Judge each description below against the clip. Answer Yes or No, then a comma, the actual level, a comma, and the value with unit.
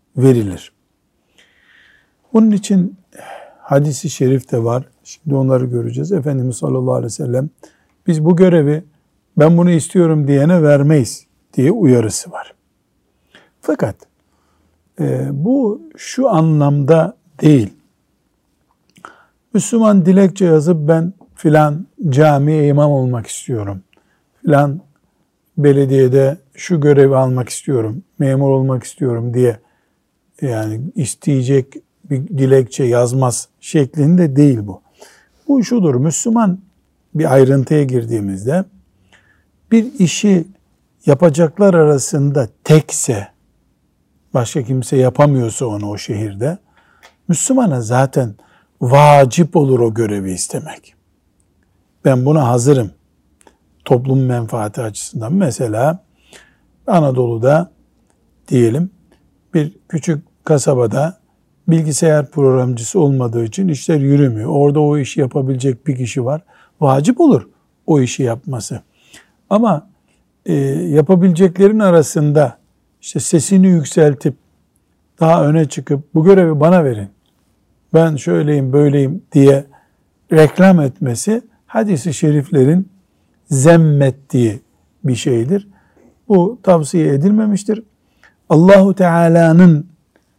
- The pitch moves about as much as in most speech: Yes, average, 4.9 semitones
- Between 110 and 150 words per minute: No, slow, 95 wpm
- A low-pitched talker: No, medium, 145 Hz